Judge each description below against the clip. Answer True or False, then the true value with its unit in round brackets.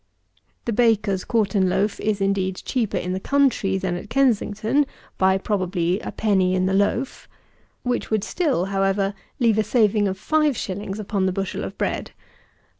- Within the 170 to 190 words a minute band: False (160 wpm)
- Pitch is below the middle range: False (200 Hz)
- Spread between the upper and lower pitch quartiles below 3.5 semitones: True (2.9 semitones)